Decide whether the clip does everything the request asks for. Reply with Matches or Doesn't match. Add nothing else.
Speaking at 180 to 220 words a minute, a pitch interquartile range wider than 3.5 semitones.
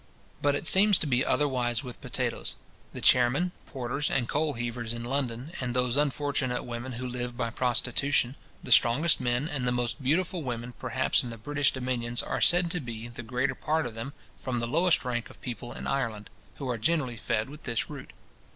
Doesn't match